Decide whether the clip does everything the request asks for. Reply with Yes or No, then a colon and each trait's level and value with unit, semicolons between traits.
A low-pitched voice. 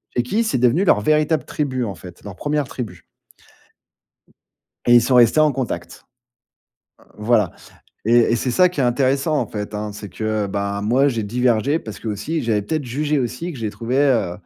Yes: low, 120 Hz